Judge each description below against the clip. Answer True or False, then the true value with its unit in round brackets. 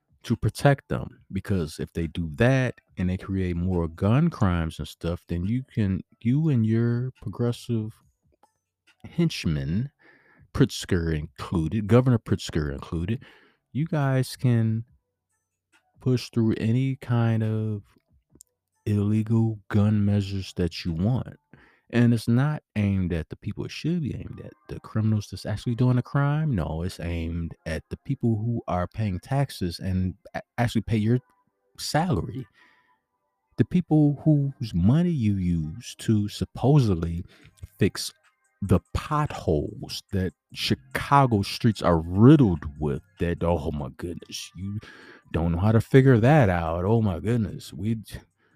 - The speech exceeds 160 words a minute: False (135 wpm)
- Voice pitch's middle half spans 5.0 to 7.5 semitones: True (5.3 semitones)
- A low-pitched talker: True (105 Hz)